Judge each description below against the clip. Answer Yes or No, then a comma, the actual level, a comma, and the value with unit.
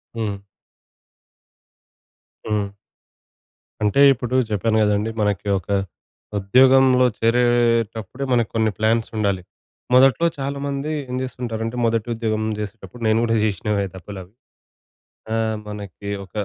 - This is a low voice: Yes, low, 110 Hz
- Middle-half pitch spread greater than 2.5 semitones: Yes, average, 2.9 semitones